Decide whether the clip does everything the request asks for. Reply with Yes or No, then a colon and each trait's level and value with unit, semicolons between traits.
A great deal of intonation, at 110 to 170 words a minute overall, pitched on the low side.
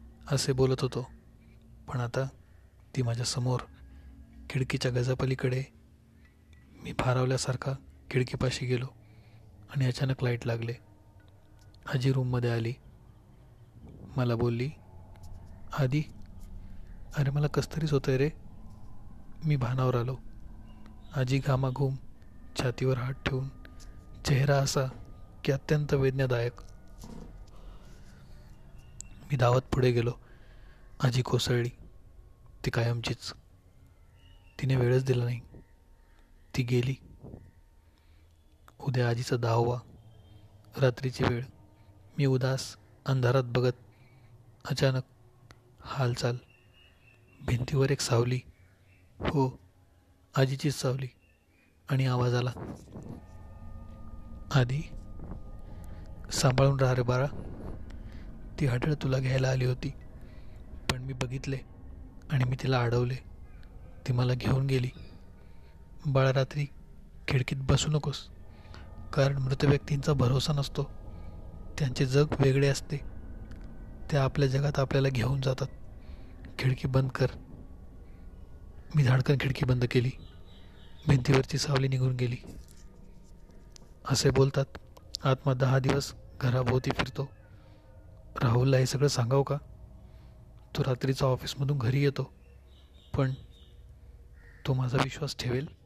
No: wide, 5.8 semitones; average, 95 wpm; low, 120 Hz